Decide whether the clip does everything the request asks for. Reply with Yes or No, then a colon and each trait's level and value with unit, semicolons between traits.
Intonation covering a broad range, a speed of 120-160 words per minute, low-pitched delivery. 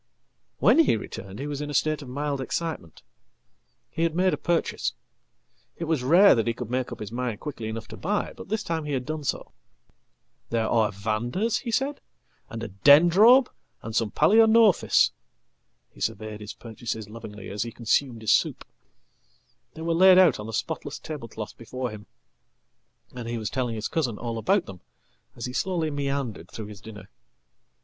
No: wide, 6.7 semitones; average, 170 wpm; low, 125 Hz